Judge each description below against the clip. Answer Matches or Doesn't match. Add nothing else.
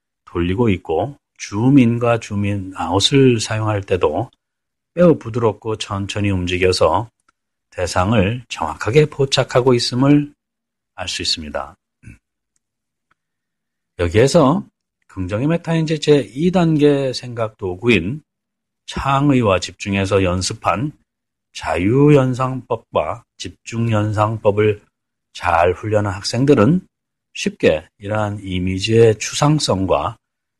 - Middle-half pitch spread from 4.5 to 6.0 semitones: Matches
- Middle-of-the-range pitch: Doesn't match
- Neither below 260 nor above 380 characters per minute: Doesn't match